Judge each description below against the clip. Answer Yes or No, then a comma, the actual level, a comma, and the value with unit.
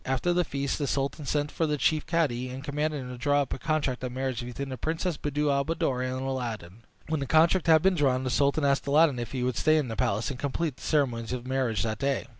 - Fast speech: Yes, fast, 260 wpm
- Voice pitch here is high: No, medium, 140 Hz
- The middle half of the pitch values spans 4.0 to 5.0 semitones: No, average, 3.2 semitones